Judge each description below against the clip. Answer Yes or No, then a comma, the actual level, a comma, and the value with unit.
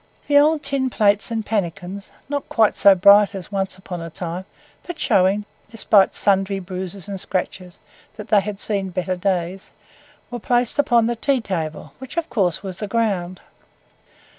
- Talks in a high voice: Yes, high, 200 Hz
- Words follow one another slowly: No, average, 165 wpm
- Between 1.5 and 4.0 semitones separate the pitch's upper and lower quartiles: Yes, average, 3.6 semitones